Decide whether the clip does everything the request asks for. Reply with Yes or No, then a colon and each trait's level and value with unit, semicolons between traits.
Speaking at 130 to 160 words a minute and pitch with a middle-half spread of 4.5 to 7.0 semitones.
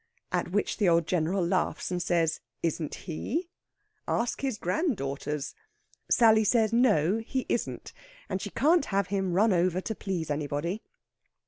Yes: average, 145 wpm; average, 5.0 semitones